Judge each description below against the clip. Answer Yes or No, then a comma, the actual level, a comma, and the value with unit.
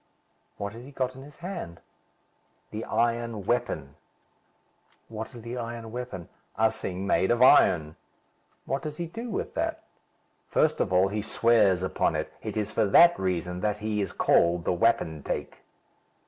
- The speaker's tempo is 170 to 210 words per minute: No, average, 160 wpm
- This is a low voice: Yes, low, 110 Hz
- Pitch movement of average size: Yes, average, 4.5 semitones